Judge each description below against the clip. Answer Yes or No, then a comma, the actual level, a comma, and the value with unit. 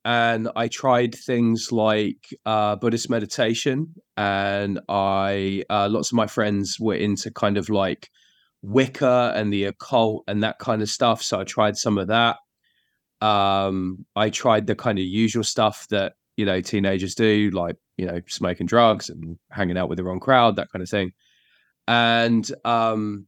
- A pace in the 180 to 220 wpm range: No, average, 170 wpm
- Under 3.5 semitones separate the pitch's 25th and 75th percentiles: Yes, average, 2.8 semitones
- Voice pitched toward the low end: Yes, low, 105 Hz